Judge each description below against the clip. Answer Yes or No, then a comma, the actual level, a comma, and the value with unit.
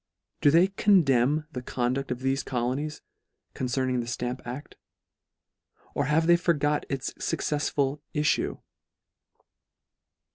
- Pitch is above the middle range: No, low, 135 Hz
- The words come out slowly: Yes, slow, 130 wpm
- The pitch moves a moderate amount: Yes, average, 3.1 semitones